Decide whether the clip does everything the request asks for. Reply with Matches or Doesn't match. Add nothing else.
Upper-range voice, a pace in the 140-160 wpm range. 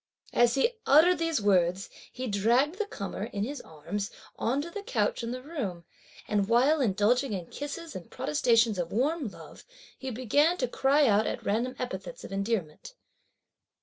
Doesn't match